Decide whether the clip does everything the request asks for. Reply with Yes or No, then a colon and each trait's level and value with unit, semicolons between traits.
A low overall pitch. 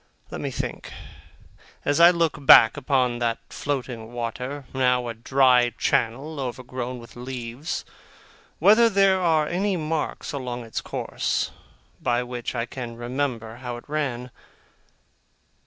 Yes: low, 125 Hz